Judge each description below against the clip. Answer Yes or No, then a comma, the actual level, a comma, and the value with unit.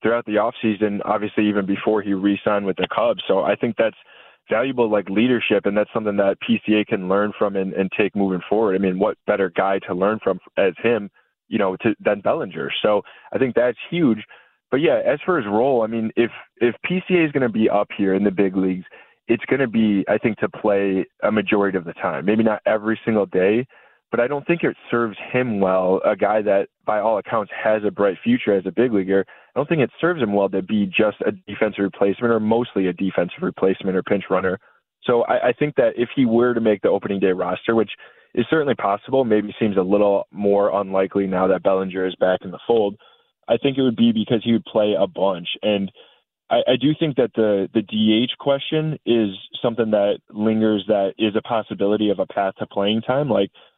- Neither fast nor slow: No, fast, 225 wpm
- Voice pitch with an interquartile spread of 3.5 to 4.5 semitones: No, average, 2.8 semitones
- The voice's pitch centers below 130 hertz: Yes, low, 105 Hz